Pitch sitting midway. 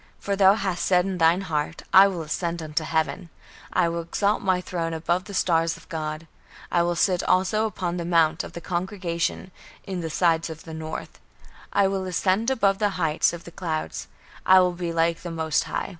Yes: medium, 175 Hz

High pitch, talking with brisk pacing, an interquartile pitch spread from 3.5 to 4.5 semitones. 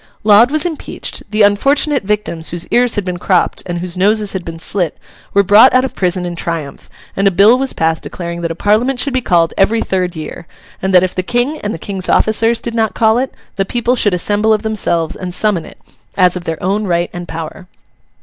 Yes: high, 195 Hz; fast, 225 wpm; average, 4.1 semitones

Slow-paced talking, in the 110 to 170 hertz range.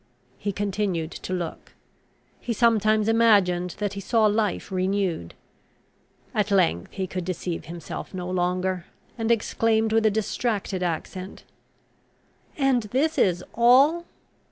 No: slow, 125 wpm; high, 200 Hz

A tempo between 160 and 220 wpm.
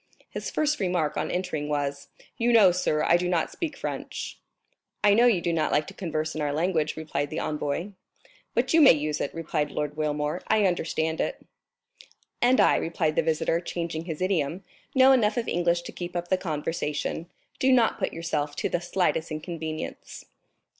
Yes: average, 185 wpm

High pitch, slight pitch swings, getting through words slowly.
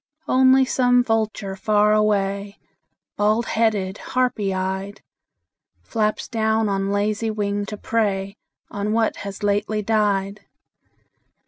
Yes: high, 210 Hz; narrow, 1.7 semitones; slow, 110 wpm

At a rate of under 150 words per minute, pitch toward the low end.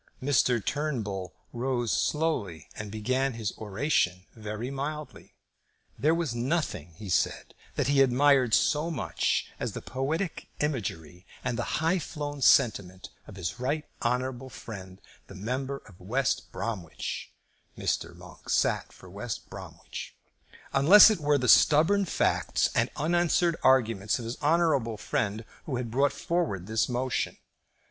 Yes: average, 140 wpm; low, 125 Hz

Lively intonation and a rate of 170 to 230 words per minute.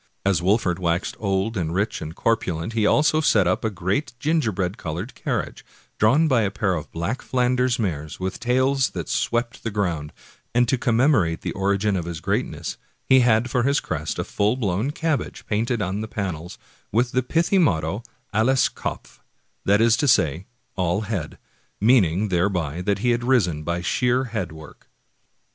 Yes: wide, 5.8 semitones; average, 175 wpm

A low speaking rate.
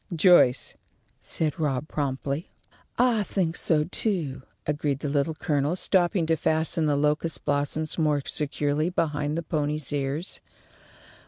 Yes: slow, 130 wpm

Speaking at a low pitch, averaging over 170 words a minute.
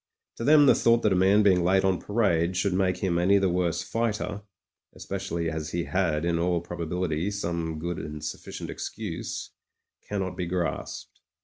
Yes: very low, 90 Hz; average, 180 wpm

